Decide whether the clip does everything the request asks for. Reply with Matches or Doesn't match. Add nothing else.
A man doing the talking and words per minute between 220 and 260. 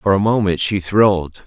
Doesn't match